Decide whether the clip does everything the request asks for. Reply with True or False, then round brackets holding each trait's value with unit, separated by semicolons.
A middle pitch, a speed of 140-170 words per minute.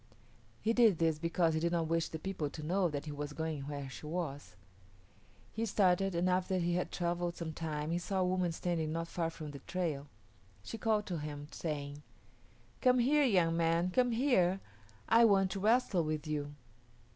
False (170 Hz; 190 wpm)